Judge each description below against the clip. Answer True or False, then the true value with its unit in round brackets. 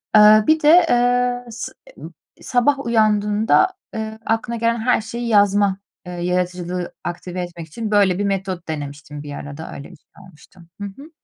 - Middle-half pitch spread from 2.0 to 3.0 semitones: False (4.7 semitones)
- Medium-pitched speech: False (205 Hz)